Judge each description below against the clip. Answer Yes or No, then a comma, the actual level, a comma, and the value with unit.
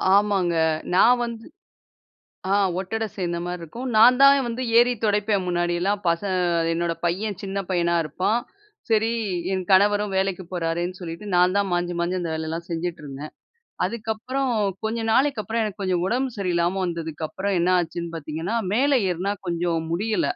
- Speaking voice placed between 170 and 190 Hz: Yes, medium, 185 Hz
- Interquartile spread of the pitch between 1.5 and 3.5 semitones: No, average, 4.0 semitones